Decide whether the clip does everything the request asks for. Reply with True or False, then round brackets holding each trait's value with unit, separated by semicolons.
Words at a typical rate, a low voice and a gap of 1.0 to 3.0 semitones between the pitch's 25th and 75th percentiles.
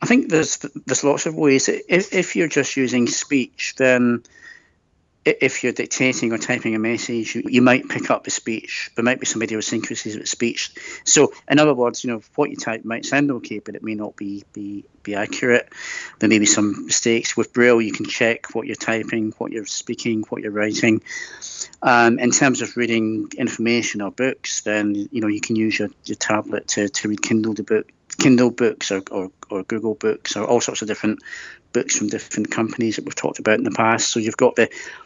False (210 wpm; 115 Hz; 2.7 semitones)